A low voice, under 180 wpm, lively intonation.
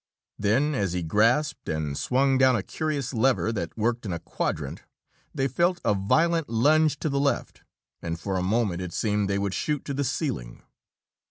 No: low, 115 Hz; average, 185 wpm; wide, 6.3 semitones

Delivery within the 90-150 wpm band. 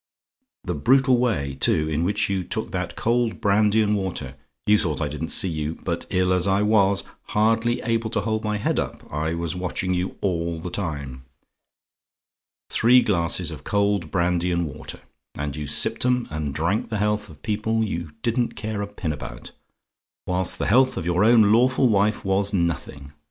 No: average, 185 wpm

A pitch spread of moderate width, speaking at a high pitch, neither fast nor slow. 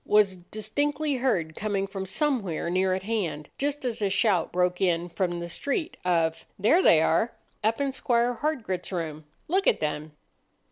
No: wide, 6.1 semitones; high, 195 Hz; average, 160 wpm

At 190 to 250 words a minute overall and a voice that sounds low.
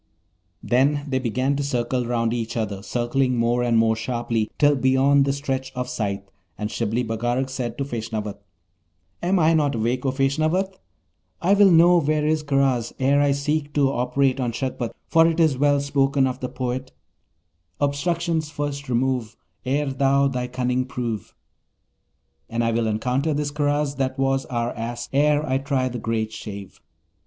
No: average, 170 wpm; low, 130 Hz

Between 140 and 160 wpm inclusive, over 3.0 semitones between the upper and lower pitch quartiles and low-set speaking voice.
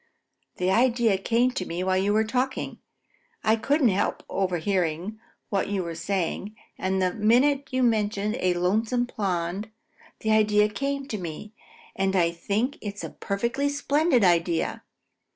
No: average, 150 wpm; average, 4.3 semitones; high, 210 Hz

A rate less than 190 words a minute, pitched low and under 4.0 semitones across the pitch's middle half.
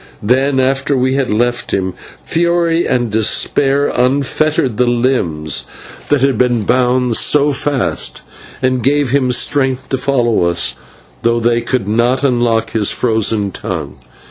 Yes: average, 140 wpm; low, 125 Hz; average, 3.0 semitones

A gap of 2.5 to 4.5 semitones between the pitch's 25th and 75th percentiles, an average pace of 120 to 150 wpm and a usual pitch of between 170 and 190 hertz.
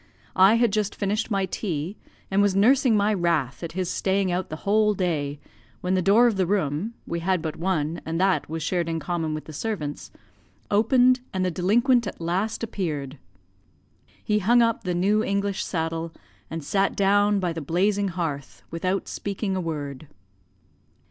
No: average, 3.9 semitones; average, 175 wpm; medium, 185 Hz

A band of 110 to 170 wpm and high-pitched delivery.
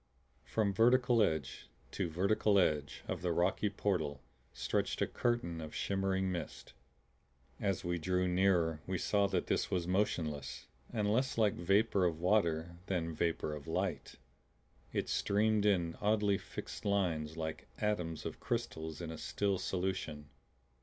No: average, 145 wpm; very low, 90 Hz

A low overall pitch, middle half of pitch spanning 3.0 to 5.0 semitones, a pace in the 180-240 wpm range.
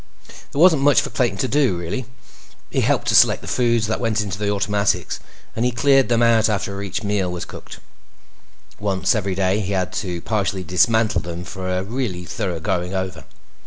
Yes: low, 100 Hz; average, 4.1 semitones; average, 195 wpm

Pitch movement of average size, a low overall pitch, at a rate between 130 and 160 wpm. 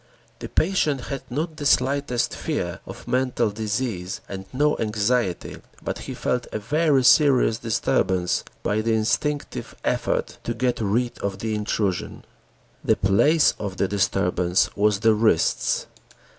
Yes: average, 4.5 semitones; low, 115 Hz; average, 140 wpm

